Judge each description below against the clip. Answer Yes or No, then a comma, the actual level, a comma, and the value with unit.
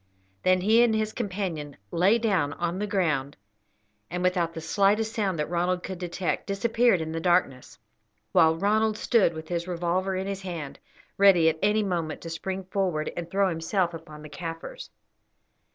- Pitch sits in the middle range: Yes, medium, 180 Hz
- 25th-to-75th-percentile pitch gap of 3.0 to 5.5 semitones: Yes, average, 3.4 semitones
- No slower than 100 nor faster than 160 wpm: No, average, 170 wpm